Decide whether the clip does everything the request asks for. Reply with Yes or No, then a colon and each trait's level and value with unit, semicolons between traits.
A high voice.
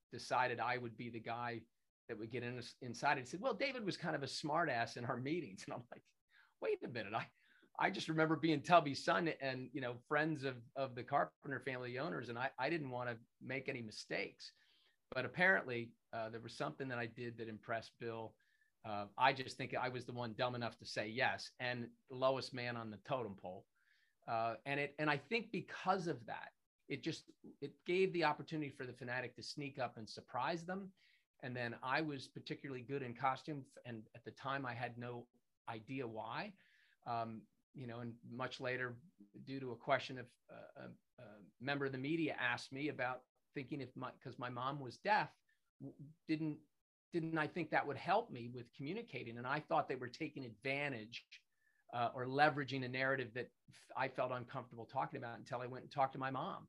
No: low, 130 Hz